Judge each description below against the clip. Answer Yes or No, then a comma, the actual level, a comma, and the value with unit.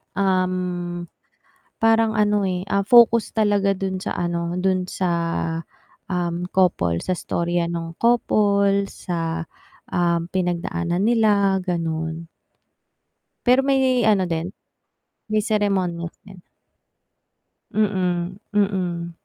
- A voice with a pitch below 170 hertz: No, medium, 185 Hz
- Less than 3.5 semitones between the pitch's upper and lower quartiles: Yes, average, 2.8 semitones